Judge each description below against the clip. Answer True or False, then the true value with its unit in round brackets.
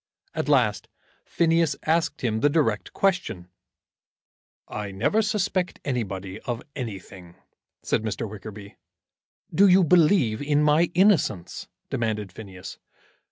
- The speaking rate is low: True (115 wpm)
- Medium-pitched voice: False (125 Hz)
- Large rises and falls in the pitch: True (8.6 semitones)